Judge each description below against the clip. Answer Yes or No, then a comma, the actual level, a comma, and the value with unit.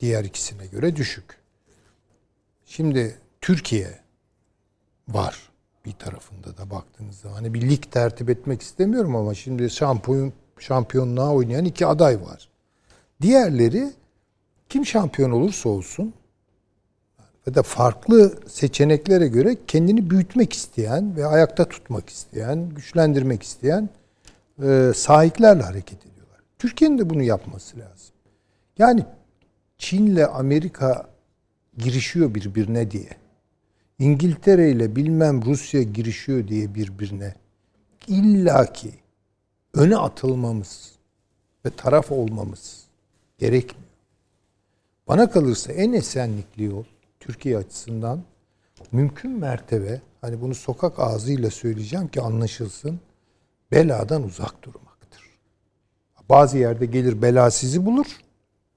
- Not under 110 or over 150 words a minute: No, average, 100 wpm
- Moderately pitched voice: No, low, 120 Hz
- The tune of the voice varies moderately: No, wide, 5.9 semitones